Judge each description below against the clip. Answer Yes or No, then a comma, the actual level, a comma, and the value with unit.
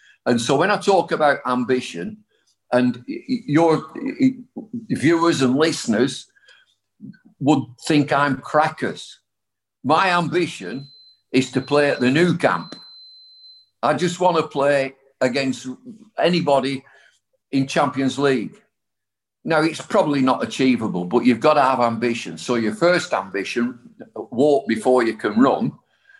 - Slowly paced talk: Yes, slow, 125 wpm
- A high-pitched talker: No, low, 135 Hz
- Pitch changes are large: Yes, wide, 6.2 semitones